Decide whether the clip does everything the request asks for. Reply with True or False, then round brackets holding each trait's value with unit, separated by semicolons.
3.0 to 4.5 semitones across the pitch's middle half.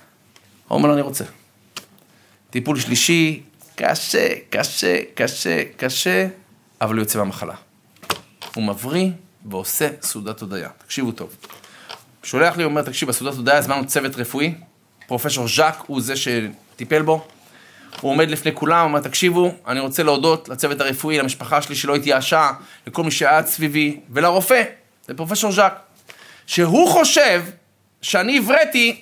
False (5.2 semitones)